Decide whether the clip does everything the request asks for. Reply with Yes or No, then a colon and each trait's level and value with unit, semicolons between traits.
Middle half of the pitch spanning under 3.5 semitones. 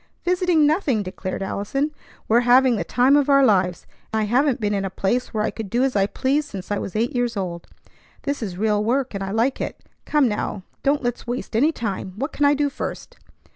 No: average, 5.3 semitones